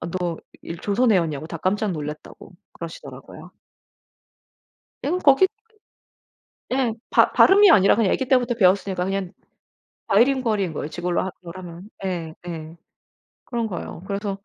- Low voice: No, high, 195 Hz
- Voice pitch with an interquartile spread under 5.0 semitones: No, average, 5.3 semitones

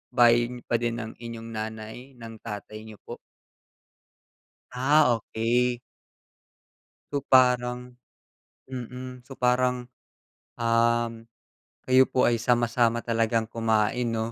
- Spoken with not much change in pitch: Yes, narrow, 1.5 semitones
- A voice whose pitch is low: Yes, low, 120 Hz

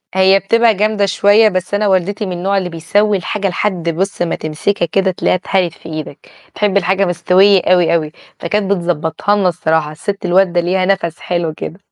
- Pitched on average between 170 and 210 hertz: Yes, medium, 185 Hz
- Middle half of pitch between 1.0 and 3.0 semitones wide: Yes, narrow, 2.6 semitones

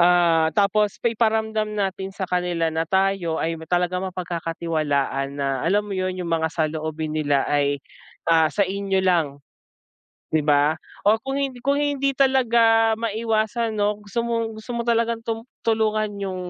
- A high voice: Yes, high, 195 Hz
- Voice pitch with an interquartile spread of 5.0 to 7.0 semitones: Yes, average, 5.3 semitones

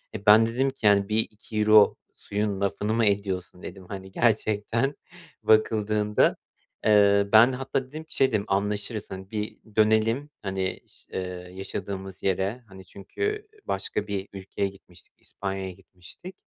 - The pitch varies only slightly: Yes, narrow, 2.3 semitones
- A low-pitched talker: Yes, low, 105 Hz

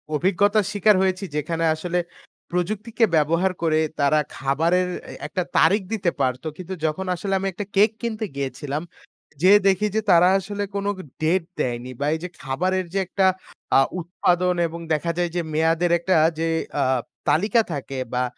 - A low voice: No, medium, 180 Hz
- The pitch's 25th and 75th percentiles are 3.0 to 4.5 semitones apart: Yes, average, 3.7 semitones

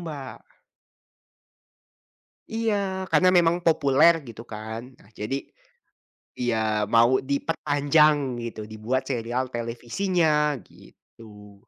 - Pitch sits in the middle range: No, low, 130 Hz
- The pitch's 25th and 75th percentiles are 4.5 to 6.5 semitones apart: Yes, wide, 5.4 semitones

